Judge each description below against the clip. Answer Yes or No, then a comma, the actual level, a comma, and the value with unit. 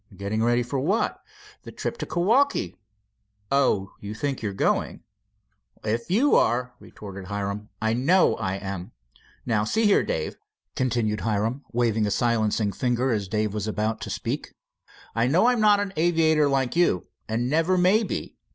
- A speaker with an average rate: Yes, average, 160 wpm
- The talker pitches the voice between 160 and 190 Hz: No, low, 120 Hz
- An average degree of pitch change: No, wide, 7.3 semitones